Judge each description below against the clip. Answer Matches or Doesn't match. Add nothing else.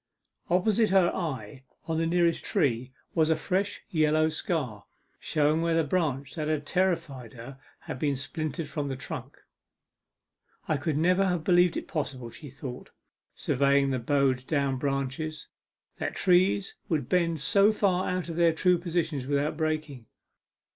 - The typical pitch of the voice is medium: Matches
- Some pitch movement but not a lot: Matches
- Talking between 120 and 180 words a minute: Matches